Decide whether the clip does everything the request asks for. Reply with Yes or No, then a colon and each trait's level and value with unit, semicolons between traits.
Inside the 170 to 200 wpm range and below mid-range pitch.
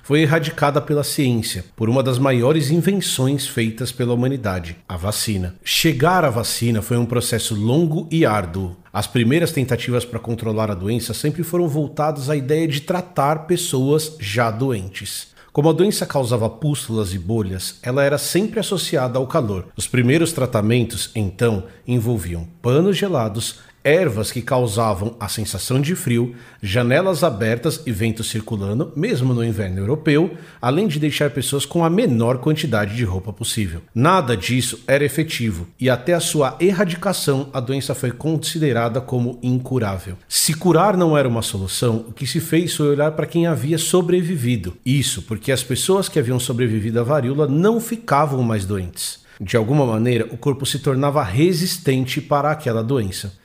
No: average, 160 wpm; low, 130 Hz